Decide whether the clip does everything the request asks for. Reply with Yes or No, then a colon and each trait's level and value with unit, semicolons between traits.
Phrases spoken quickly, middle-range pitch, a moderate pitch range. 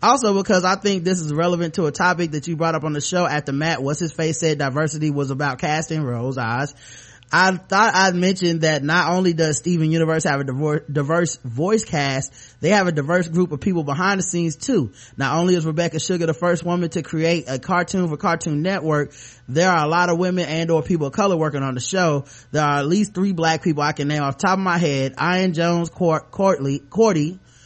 Yes: fast, 230 wpm; medium, 165 Hz; average, 3.4 semitones